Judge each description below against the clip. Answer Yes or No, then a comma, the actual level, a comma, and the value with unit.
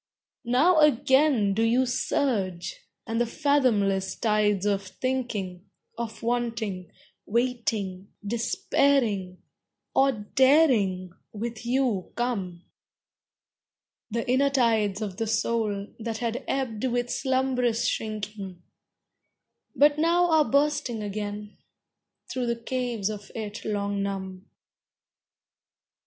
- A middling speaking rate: No, slow, 100 wpm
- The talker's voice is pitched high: Yes, high, 225 Hz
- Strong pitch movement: No, average, 4.1 semitones